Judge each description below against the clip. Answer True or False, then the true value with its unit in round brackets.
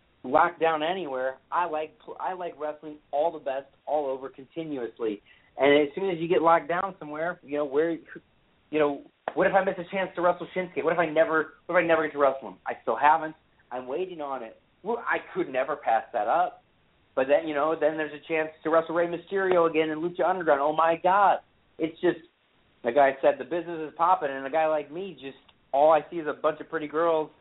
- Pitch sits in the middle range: True (155 Hz)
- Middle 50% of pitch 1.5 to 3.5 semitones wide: True (2.8 semitones)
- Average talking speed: False (230 wpm)